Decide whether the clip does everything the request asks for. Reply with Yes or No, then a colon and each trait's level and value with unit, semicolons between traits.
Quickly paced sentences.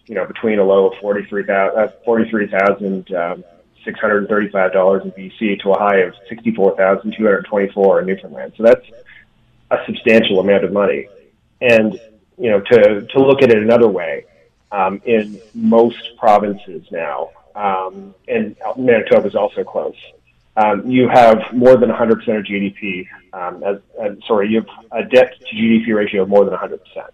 No: average, 155 wpm